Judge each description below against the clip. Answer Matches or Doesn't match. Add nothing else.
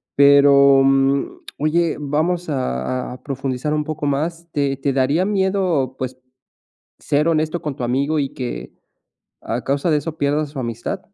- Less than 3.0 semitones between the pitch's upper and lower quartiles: Matches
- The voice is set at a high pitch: Doesn't match